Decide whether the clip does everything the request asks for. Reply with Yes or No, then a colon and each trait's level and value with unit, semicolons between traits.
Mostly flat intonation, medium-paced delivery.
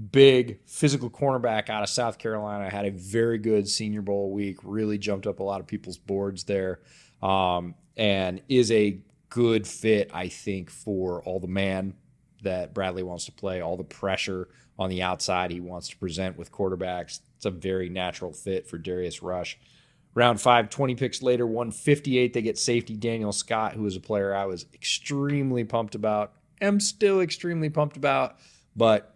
No: average, 4.4 semitones; average, 175 wpm